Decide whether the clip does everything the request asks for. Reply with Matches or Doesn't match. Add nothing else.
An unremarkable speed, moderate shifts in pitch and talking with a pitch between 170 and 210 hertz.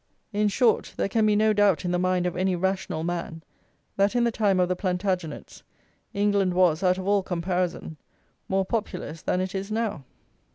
Doesn't match